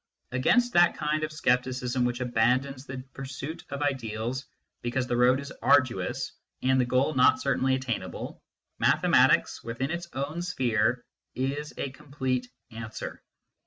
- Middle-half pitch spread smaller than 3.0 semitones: Yes, narrow, 2.5 semitones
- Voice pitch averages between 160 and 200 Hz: No, low, 130 Hz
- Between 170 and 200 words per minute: No, average, 140 wpm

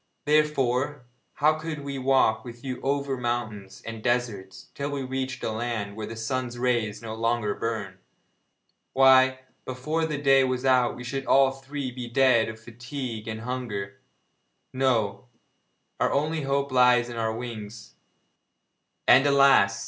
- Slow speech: No, average, 150 wpm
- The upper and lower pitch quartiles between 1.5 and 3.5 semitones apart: Yes, average, 3.2 semitones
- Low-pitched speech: Yes, low, 125 Hz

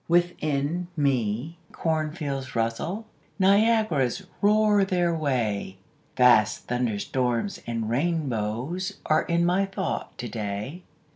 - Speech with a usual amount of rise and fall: No, wide, 6.9 semitones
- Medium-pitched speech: Yes, medium, 150 Hz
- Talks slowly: Yes, slow, 95 wpm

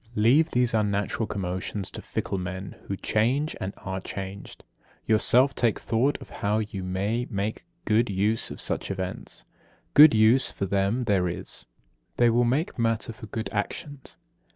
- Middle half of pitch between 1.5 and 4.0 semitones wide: Yes, average, 3.5 semitones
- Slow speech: No, average, 155 wpm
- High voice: No, low, 110 Hz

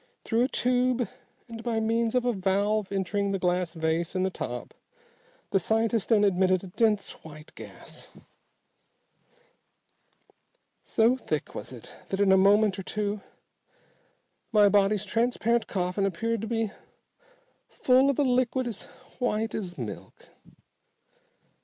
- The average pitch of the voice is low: No, high, 210 Hz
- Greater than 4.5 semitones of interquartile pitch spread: No, average, 3.3 semitones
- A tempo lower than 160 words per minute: Yes, slow, 135 wpm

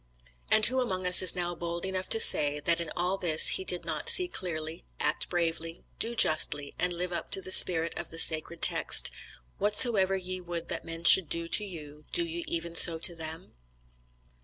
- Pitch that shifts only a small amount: Yes, narrow, 2.2 semitones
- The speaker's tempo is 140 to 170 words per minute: No, average, 200 wpm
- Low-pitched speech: No, medium, 170 Hz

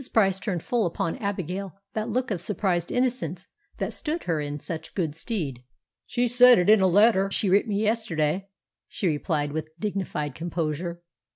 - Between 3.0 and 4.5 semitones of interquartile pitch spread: No, average, 4.9 semitones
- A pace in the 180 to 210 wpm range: No, average, 170 wpm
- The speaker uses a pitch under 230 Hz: Yes, high, 190 Hz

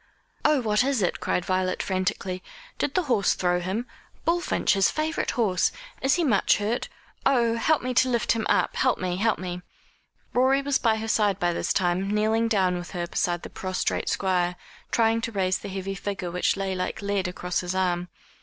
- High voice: Yes, high, 195 Hz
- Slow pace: No, average, 195 wpm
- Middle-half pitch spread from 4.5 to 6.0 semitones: No, average, 4.1 semitones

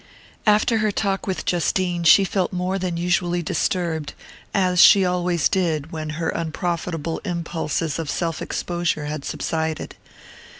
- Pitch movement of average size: No, narrow, 2.2 semitones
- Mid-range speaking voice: Yes, medium, 175 Hz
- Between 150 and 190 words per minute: No, slow, 135 wpm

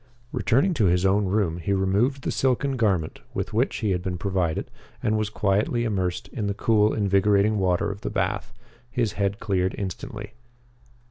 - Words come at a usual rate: Yes, average, 175 wpm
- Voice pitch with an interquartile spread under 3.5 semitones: Yes, narrow, 2.4 semitones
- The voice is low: Yes, low, 100 Hz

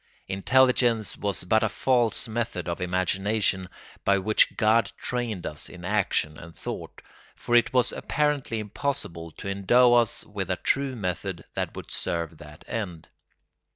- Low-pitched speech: Yes, low, 105 Hz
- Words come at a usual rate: Yes, average, 150 wpm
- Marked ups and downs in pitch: No, average, 4.8 semitones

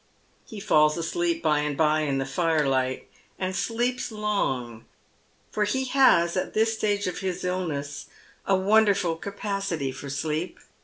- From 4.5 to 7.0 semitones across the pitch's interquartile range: Yes, wide, 5.4 semitones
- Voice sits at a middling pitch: Yes, medium, 175 Hz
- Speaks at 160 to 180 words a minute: No, average, 145 wpm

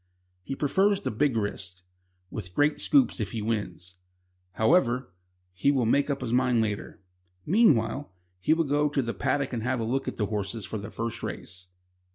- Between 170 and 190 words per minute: Yes, average, 185 wpm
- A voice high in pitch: No, low, 120 Hz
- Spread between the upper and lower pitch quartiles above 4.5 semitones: Yes, wide, 5.5 semitones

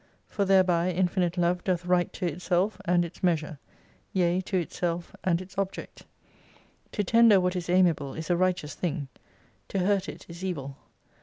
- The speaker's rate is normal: Yes, average, 170 wpm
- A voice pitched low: No, medium, 180 Hz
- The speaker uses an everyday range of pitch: No, narrow, 1.6 semitones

